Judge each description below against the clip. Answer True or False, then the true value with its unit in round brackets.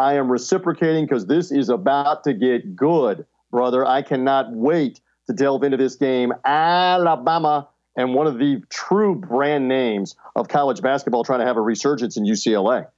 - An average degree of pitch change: True (4.2 semitones)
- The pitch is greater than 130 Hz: True (140 Hz)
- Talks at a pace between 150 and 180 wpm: True (170 wpm)